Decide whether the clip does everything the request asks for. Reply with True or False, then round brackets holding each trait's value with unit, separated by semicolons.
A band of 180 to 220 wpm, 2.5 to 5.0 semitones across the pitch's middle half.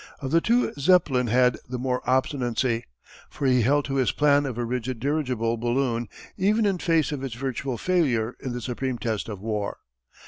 True (185 wpm; 3.2 semitones)